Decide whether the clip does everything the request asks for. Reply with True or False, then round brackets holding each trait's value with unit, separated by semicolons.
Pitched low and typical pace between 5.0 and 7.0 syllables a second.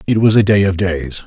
True (95 Hz; 5.3 syllables/s)